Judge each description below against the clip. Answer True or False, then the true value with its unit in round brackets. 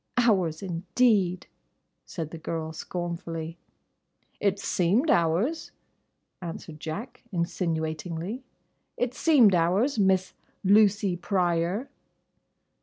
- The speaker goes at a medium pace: False (75 wpm)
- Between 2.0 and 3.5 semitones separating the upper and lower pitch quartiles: False (3.9 semitones)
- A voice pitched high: False (180 Hz)